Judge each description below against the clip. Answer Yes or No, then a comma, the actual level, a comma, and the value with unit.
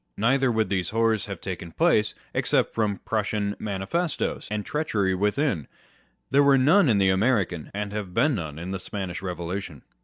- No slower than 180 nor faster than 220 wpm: No, average, 165 wpm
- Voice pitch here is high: No, low, 105 Hz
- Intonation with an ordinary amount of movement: Yes, average, 4.3 semitones